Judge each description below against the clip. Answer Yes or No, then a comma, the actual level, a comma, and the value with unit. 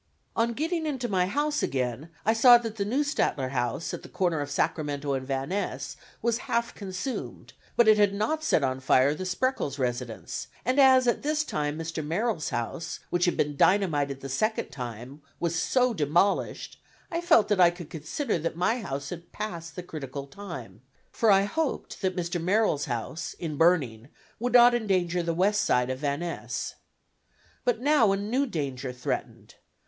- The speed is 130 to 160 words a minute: No, average, 180 wpm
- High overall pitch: No, medium, 175 Hz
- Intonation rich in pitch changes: Yes, wide, 8.2 semitones